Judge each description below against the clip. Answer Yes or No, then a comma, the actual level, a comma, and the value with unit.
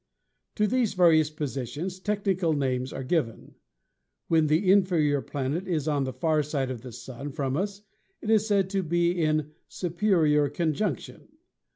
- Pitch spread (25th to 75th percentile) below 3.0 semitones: No, average, 4.8 semitones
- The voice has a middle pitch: Yes, medium, 155 Hz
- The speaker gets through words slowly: No, average, 155 wpm